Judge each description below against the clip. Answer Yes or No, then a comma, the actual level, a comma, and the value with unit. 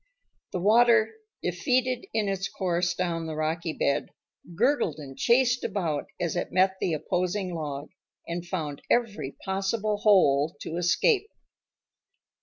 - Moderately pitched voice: Yes, medium, 180 Hz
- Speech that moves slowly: Yes, slow, 130 wpm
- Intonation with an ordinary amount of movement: Yes, average, 4.8 semitones